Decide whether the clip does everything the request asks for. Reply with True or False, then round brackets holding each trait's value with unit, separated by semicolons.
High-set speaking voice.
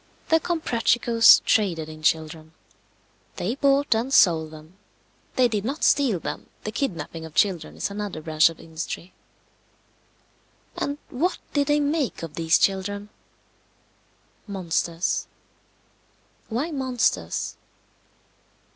True (205 Hz)